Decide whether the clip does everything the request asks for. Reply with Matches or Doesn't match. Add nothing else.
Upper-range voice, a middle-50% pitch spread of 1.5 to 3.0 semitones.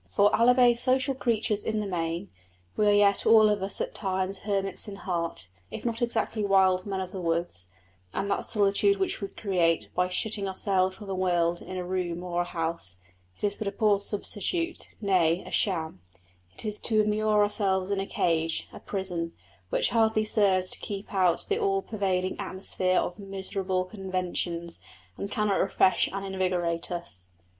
Matches